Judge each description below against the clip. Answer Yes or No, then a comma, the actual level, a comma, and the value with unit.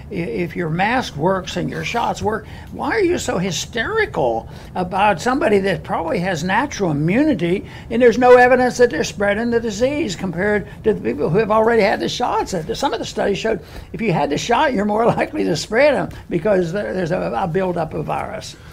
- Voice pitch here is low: No, high, 210 Hz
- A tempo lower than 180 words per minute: No, average, 195 wpm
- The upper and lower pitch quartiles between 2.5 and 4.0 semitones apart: No, average, 4.8 semitones